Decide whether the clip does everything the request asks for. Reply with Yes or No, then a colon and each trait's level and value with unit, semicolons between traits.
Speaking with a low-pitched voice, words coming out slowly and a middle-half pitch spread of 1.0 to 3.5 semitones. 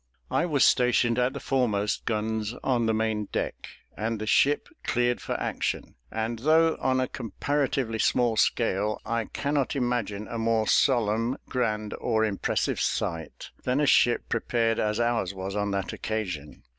No: low, 115 Hz; average, 155 wpm; average, 2.7 semitones